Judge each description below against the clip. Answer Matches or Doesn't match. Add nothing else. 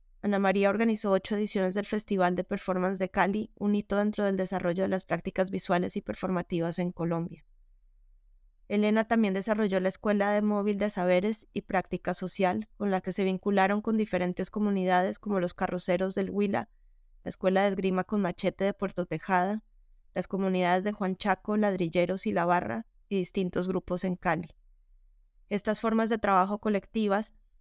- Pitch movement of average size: Doesn't match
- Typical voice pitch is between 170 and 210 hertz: Matches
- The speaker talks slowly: Doesn't match